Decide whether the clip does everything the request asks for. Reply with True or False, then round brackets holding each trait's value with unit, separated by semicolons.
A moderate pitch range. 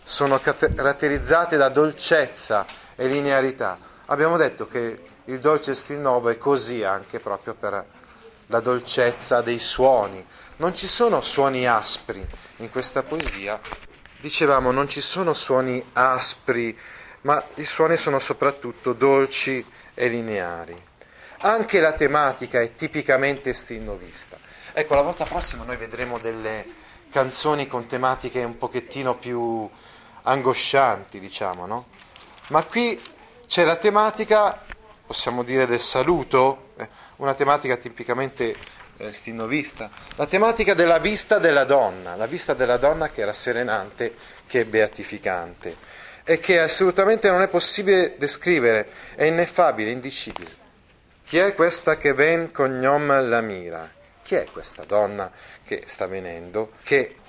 True (4.7 semitones)